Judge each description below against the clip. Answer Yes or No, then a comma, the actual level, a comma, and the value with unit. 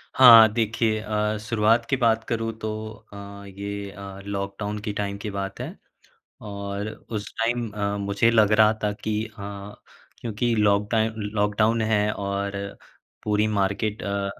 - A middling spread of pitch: No, narrow, 1.7 semitones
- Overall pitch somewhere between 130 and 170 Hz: No, low, 105 Hz